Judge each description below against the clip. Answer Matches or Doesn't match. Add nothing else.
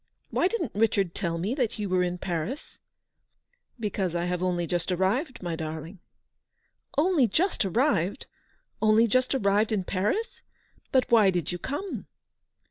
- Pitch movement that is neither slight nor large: Doesn't match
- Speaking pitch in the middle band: Doesn't match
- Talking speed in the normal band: Matches